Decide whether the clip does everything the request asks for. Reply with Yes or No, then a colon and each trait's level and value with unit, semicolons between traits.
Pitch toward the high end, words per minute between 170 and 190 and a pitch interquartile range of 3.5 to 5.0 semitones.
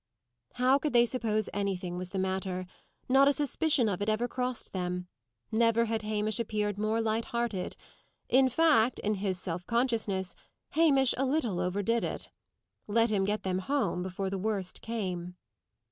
No: high, 215 Hz; average, 160 wpm; average, 4.1 semitones